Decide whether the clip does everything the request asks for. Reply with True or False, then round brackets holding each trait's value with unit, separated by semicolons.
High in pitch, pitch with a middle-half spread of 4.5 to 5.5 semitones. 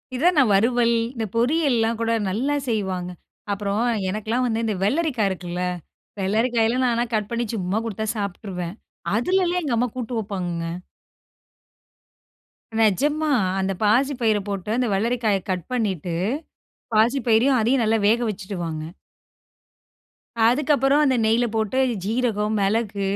False (225 Hz; 3.8 semitones)